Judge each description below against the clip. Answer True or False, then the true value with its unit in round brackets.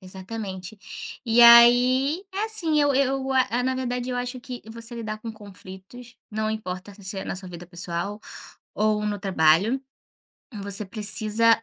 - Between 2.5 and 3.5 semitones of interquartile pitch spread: False (4.2 semitones)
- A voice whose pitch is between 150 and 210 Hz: False (220 Hz)